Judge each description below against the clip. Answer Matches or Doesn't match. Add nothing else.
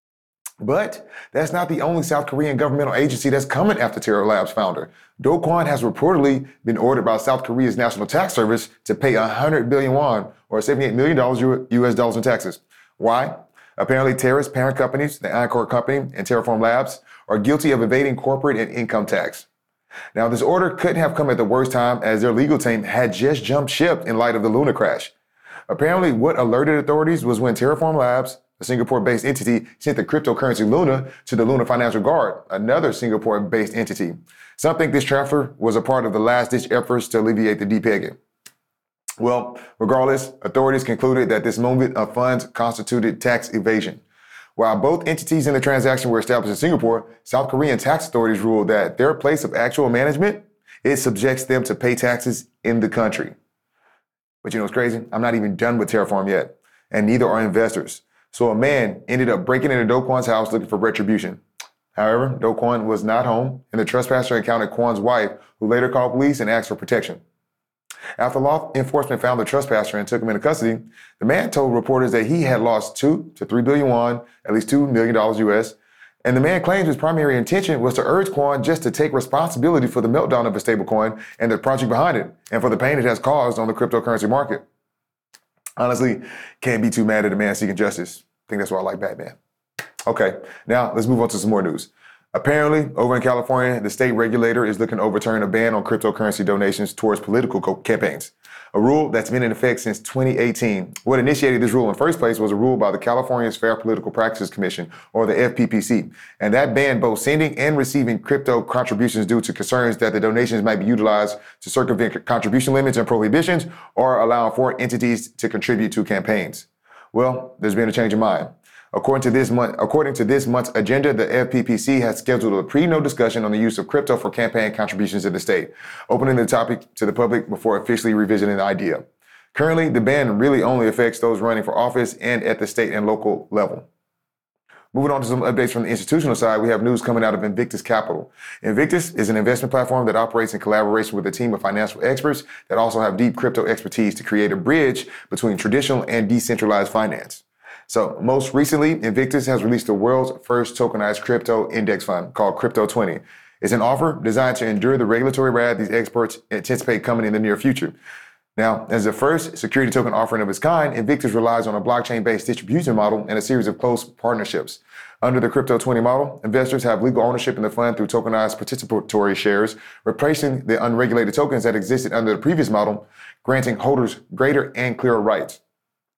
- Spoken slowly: Doesn't match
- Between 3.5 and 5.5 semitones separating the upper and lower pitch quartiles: Doesn't match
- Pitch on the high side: Doesn't match